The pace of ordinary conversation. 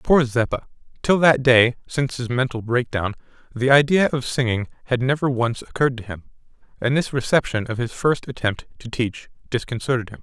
Yes: average, 180 wpm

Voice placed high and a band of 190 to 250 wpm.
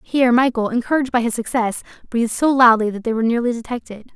Yes: high, 240 Hz; average, 200 wpm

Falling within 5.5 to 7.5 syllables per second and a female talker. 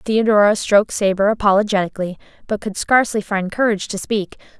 Yes: 6.1 syllables/s; female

